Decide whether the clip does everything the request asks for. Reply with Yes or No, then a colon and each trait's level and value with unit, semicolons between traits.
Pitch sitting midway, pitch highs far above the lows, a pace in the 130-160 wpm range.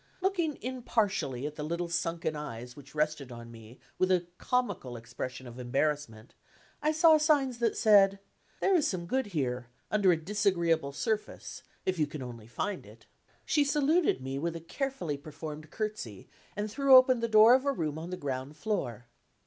No: medium, 170 Hz; wide, 8.9 semitones; average, 175 wpm